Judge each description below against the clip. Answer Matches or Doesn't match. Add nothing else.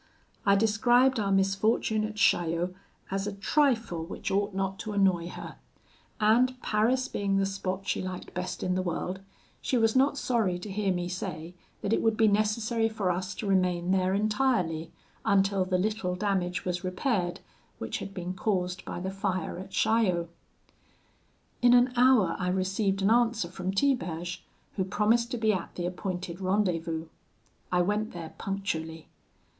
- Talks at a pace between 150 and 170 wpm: Matches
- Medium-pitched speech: Doesn't match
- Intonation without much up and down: Doesn't match